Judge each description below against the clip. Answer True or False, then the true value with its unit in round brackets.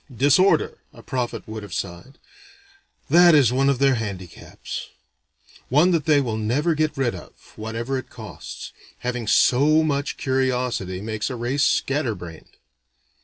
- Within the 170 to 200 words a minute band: False (145 wpm)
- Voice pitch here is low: True (130 Hz)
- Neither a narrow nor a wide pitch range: True (4.6 semitones)